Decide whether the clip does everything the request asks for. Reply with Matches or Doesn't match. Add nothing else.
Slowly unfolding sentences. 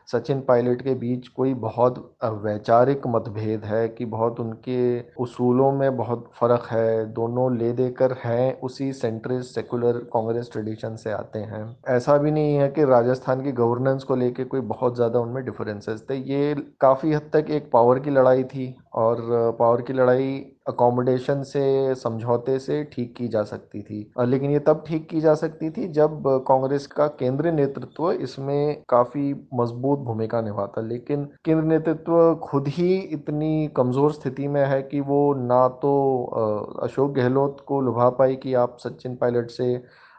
Doesn't match